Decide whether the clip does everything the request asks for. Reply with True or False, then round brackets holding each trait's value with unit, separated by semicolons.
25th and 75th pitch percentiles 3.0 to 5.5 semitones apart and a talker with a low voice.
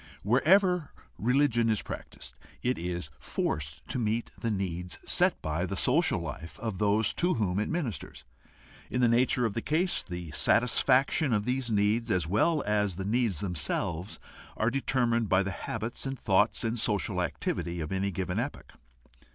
True (5.1 semitones; 110 Hz)